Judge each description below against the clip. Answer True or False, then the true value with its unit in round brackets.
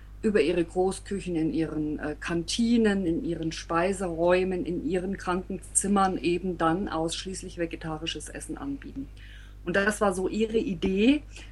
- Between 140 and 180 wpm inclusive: False (125 wpm)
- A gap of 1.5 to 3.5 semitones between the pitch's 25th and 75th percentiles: True (3.1 semitones)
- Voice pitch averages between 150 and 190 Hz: True (185 Hz)